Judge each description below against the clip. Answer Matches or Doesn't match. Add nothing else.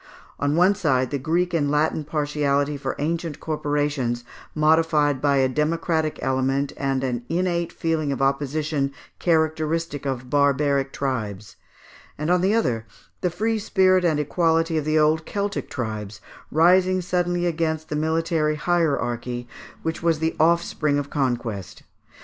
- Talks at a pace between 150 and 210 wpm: Doesn't match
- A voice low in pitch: Doesn't match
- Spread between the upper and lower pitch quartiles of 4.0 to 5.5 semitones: Doesn't match